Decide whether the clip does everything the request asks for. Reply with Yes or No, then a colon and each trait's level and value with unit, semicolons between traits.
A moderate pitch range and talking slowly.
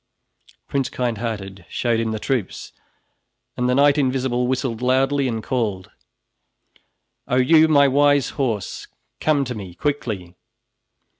Yes: average, 3.8 semitones; slow, 125 wpm